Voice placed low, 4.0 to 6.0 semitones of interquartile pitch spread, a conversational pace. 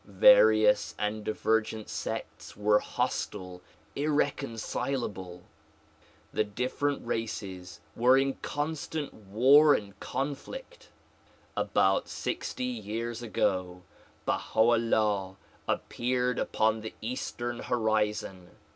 No: low, 115 Hz; average, 4.7 semitones; slow, 85 wpm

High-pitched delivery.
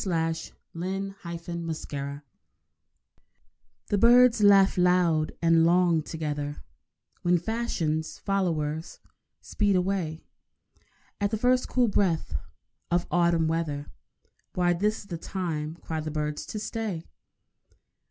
No: medium, 170 Hz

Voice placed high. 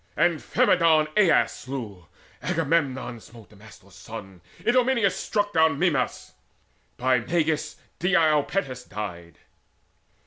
No: medium, 140 Hz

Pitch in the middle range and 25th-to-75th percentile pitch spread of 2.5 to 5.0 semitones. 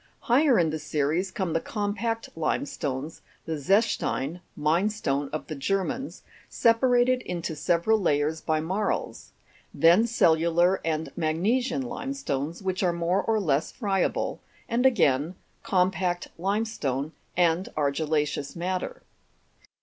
No: medium, 175 Hz; wide, 5.5 semitones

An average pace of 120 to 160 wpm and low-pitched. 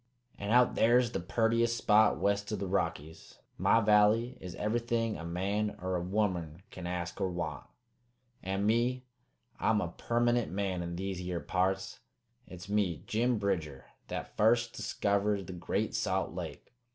Yes: average, 155 wpm; low, 100 Hz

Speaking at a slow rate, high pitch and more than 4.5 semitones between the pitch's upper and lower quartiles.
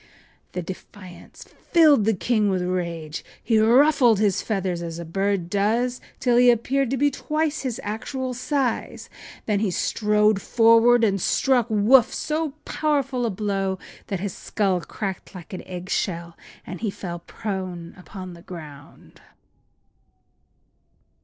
No: average, 145 wpm; high, 210 Hz; average, 4.9 semitones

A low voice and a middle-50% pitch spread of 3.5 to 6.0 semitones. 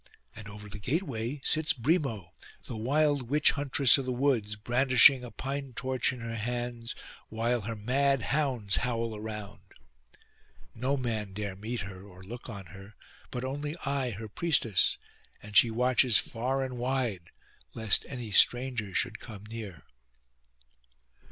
Yes: low, 120 Hz; average, 3.8 semitones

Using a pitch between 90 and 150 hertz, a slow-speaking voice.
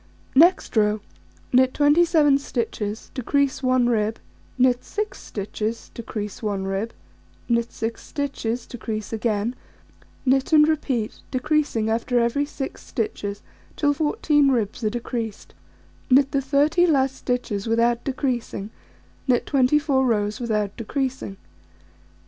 No: high, 245 Hz; slow, 120 wpm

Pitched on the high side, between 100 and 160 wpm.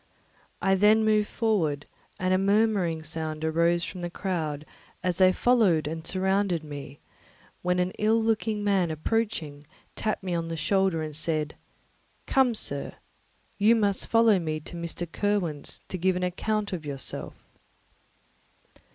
No: medium, 180 Hz; average, 145 wpm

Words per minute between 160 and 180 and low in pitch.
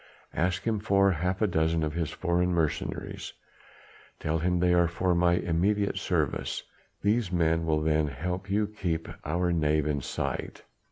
Yes: average, 165 wpm; very low, 85 Hz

